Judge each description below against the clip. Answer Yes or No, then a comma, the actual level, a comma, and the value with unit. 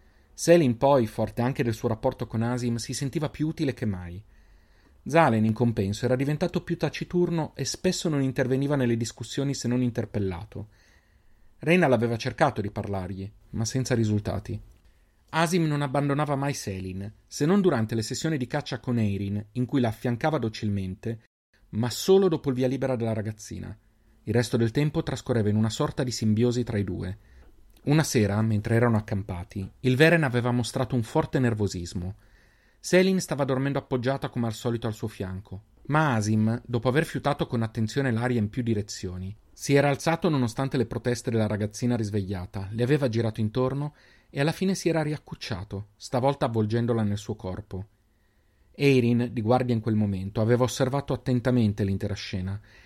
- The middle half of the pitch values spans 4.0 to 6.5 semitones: Yes, average, 4.7 semitones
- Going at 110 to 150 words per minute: No, average, 165 wpm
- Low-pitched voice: Yes, low, 120 Hz